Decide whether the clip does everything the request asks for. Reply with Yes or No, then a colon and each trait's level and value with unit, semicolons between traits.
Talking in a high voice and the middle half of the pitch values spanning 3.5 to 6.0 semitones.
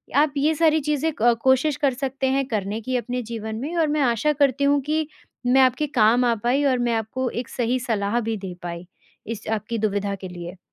Yes: very high, 250 Hz; average, 4.4 semitones